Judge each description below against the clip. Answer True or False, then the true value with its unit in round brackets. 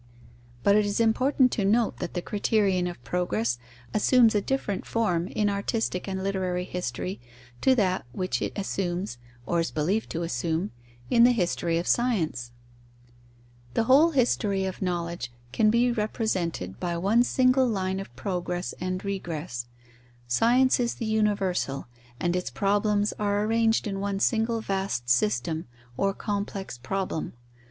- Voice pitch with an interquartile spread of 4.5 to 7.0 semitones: False (4.1 semitones)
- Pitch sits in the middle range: False (195 Hz)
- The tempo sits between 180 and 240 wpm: False (145 wpm)